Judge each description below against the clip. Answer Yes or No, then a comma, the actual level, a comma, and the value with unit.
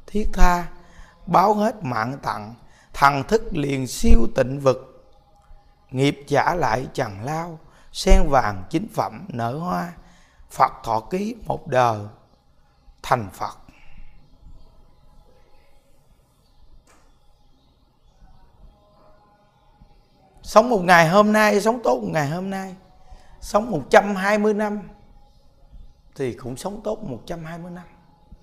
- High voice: No, medium, 140 Hz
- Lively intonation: Yes, wide, 8.9 semitones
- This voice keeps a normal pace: No, slow, 105 wpm